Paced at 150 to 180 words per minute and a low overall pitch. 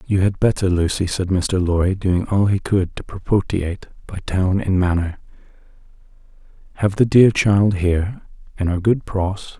Yes: average, 165 wpm; very low, 95 Hz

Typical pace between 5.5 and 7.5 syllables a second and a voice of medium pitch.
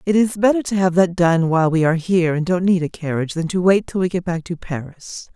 Yes: 6.1 syllables/s; medium, 175 Hz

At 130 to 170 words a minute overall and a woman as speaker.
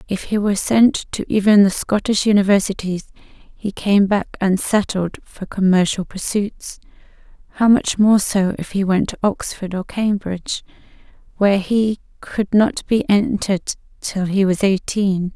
Yes: average, 145 wpm; female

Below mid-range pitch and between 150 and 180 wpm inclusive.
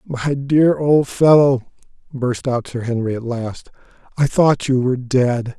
Yes: low, 130 Hz; average, 160 wpm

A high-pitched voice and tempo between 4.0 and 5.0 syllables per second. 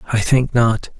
No: low, 120 Hz; 4.2 syllables/s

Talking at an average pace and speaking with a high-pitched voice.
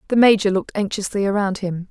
Yes: average, 190 wpm; high, 200 Hz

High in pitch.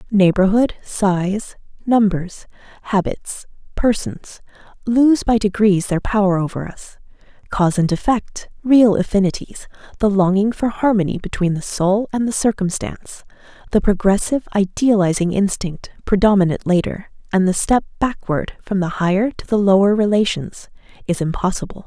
Yes: high, 200 Hz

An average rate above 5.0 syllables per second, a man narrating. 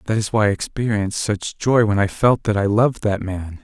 Yes: 5.5 syllables/s; male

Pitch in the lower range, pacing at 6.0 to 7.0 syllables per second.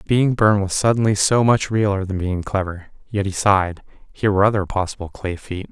No: low, 100 Hz; 5.7 syllables/s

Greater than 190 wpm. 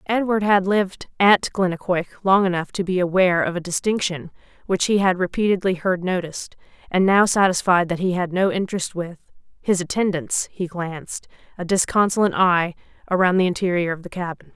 No: average, 170 wpm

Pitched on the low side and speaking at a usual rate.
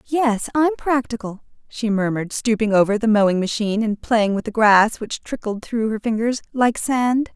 No: high, 225 Hz; average, 180 wpm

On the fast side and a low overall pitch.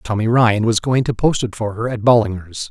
Yes: fast, 245 wpm; low, 115 Hz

